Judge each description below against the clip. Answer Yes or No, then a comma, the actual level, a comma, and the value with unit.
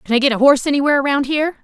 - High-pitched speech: Yes, very high, 275 Hz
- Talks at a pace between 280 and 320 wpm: Yes, fast, 295 wpm